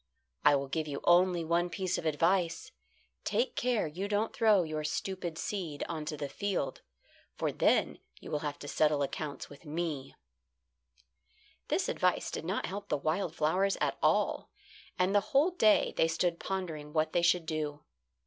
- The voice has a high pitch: No, medium, 170 Hz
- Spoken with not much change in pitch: No, average, 3.9 semitones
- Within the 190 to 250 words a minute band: No, average, 170 wpm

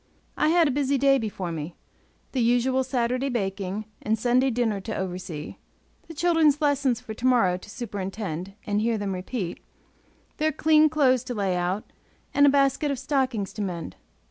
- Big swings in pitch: Yes, wide, 5.8 semitones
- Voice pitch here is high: Yes, high, 240 Hz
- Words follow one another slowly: No, average, 170 wpm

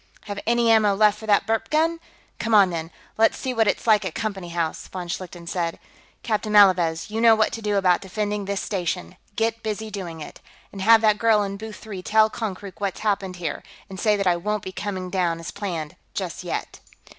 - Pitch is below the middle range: No, high, 205 Hz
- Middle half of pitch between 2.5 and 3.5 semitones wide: Yes, average, 3.0 semitones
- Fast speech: Yes, fast, 215 wpm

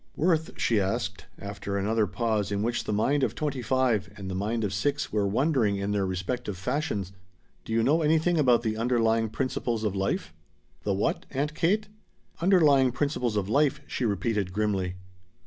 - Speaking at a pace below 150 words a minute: No, average, 175 wpm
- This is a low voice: Yes, low, 115 Hz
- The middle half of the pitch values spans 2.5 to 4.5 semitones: No, wide, 5.5 semitones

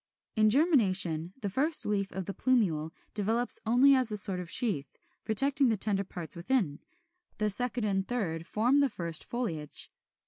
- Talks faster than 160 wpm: Yes, average, 170 wpm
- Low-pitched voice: No, high, 210 Hz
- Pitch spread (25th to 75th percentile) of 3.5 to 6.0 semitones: Yes, average, 5.3 semitones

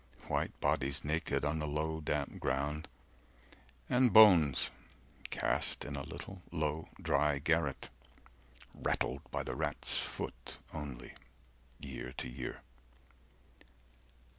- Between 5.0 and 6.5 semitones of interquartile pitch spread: No, narrow, 2.6 semitones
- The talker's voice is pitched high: No, very low, 75 Hz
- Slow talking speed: Yes, slow, 110 wpm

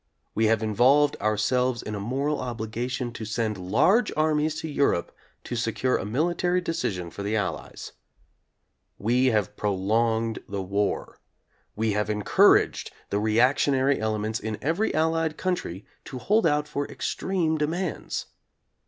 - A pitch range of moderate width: No, wide, 5.8 semitones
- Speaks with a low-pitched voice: Yes, low, 120 Hz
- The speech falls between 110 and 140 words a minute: Yes, slow, 135 wpm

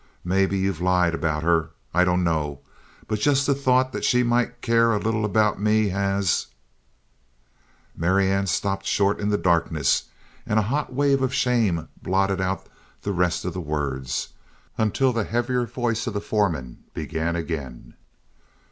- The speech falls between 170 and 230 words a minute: No, average, 155 wpm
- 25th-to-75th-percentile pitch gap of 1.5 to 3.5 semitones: No, average, 5.3 semitones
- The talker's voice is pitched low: Yes, very low, 95 Hz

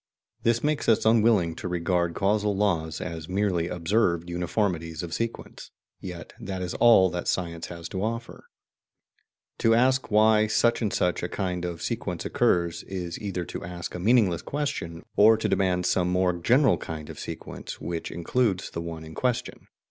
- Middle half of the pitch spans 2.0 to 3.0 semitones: No, average, 4.3 semitones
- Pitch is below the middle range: Yes, very low, 90 Hz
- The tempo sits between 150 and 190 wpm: Yes, average, 170 wpm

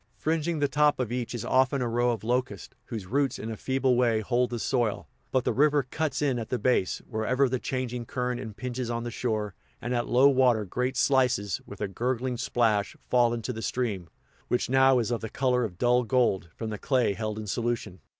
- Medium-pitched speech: No, low, 125 Hz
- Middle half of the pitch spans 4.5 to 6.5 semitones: No, narrow, 2.5 semitones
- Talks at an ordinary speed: No, fast, 215 wpm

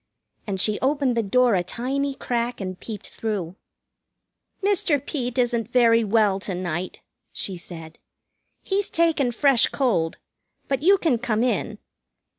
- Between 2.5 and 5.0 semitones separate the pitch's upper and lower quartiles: No, wide, 5.6 semitones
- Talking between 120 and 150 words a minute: Yes, average, 140 wpm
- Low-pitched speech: No, high, 235 Hz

